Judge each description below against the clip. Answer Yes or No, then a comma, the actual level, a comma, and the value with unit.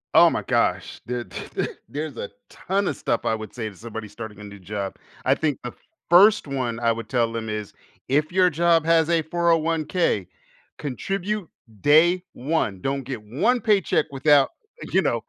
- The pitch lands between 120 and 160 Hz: Yes, medium, 140 Hz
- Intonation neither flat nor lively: No, wide, 6.8 semitones